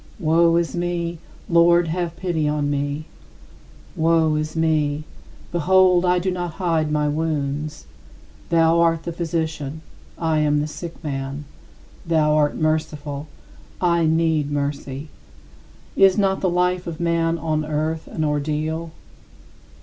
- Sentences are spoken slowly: Yes, slow, 130 wpm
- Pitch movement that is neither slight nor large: No, narrow, 2.0 semitones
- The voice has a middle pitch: Yes, medium, 160 Hz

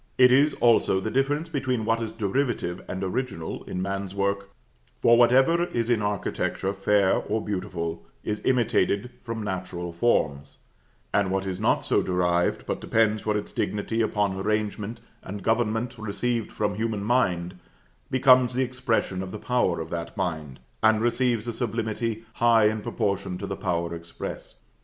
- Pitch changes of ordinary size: Yes, average, 3.8 semitones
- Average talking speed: Yes, average, 160 wpm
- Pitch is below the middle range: Yes, low, 105 Hz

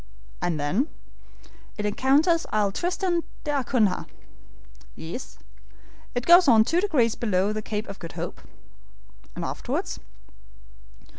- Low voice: No, high, 230 Hz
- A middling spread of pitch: No, wide, 7.5 semitones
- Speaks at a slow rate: Yes, slow, 115 wpm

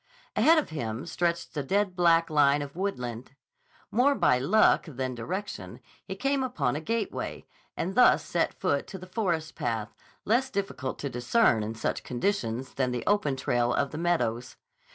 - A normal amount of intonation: No, wide, 8.1 semitones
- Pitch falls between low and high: Yes, medium, 155 Hz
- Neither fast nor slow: Yes, average, 170 wpm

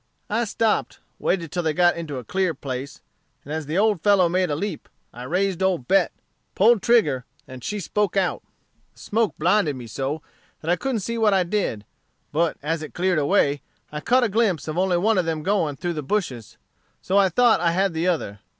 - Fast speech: Yes, fast, 210 wpm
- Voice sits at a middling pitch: Yes, medium, 175 Hz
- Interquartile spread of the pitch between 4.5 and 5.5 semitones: Yes, average, 5.0 semitones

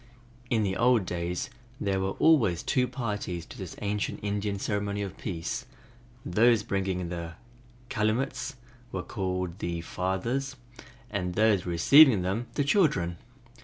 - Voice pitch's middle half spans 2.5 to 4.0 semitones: No, average, 4.6 semitones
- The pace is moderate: No, slow, 130 wpm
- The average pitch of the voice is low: Yes, low, 100 Hz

